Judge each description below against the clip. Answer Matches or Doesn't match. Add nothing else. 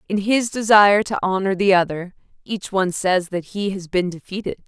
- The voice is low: Doesn't match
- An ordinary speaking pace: Matches